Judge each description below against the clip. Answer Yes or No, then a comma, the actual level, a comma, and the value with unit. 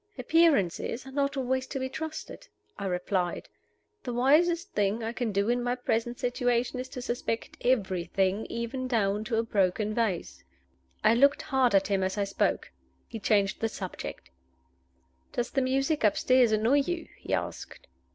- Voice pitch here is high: Yes, high, 235 Hz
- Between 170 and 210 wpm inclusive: No, average, 160 wpm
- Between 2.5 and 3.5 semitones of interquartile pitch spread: No, average, 4.3 semitones